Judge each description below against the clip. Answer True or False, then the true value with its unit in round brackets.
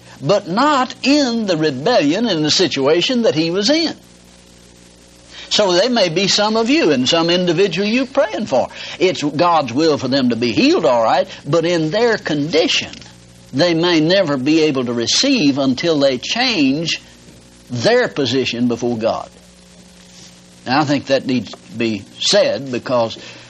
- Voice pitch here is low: False (155 Hz)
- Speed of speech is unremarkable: True (160 wpm)